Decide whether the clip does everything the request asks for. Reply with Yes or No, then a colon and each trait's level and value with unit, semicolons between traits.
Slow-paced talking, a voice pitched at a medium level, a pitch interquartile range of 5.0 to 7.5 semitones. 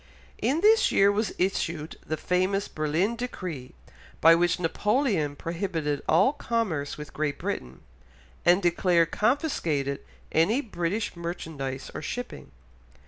Yes: slow, 120 wpm; medium, 175 Hz; average, 5.3 semitones